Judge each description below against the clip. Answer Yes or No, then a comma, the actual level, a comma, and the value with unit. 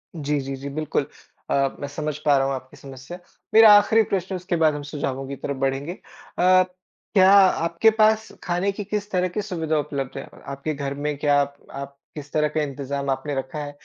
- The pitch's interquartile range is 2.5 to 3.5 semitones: No, average, 4.6 semitones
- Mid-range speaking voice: Yes, medium, 150 Hz